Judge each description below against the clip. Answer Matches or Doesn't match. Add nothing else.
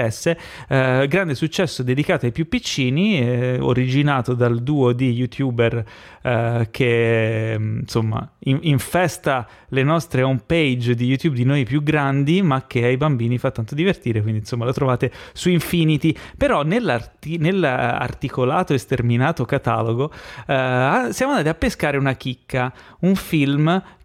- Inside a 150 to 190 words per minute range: Doesn't match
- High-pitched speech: Doesn't match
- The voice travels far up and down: Doesn't match